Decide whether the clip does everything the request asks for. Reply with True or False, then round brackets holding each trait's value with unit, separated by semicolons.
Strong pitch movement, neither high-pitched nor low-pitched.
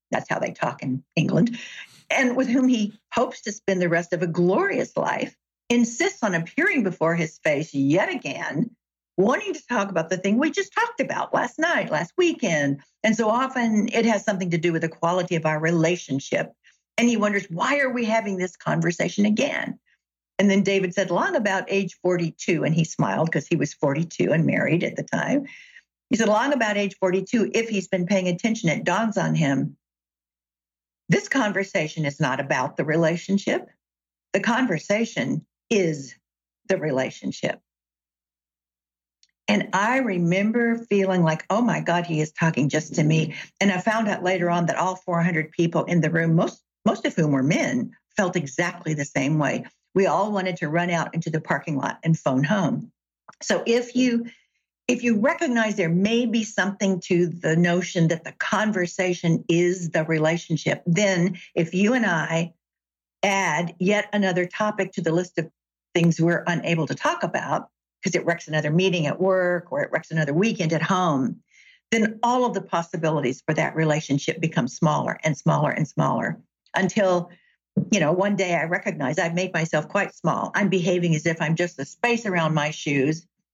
False (4.7 semitones; 180 Hz)